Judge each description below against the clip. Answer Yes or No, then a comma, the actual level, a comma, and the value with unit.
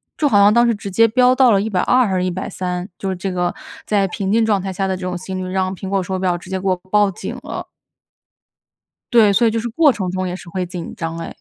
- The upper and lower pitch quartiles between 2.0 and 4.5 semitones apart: Yes, average, 2.8 semitones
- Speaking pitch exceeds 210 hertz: No, high, 190 Hz